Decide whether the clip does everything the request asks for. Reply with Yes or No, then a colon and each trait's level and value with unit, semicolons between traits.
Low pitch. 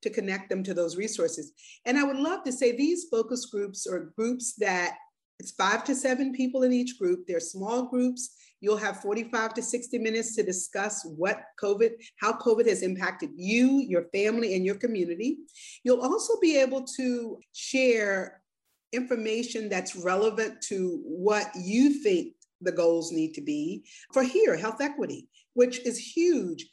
No: high, 230 Hz